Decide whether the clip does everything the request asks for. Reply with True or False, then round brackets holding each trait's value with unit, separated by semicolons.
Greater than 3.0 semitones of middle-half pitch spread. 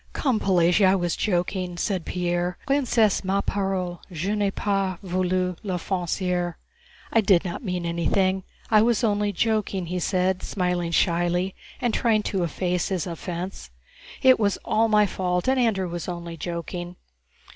False (2.6 semitones)